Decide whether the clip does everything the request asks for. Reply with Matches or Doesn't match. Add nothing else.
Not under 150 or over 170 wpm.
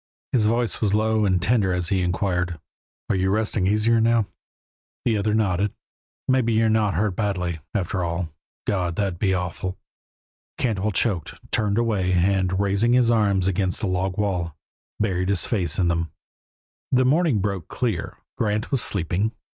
Matches